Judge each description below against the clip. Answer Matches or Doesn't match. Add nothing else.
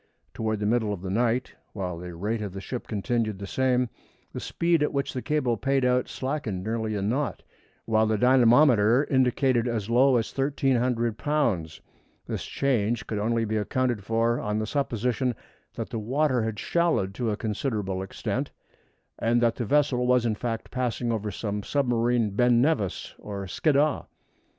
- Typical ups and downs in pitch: Matches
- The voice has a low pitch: Matches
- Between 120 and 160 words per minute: Doesn't match